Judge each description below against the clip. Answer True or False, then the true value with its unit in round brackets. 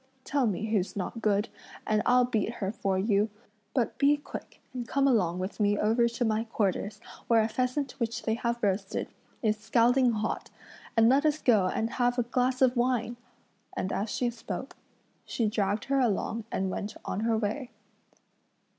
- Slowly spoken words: False (180 wpm)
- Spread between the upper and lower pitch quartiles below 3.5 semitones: True (2.9 semitones)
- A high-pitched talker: True (225 Hz)